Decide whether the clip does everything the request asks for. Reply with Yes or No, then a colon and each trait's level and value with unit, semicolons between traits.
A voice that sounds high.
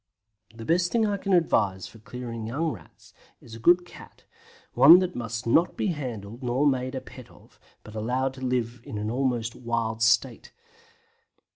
No: low, 125 Hz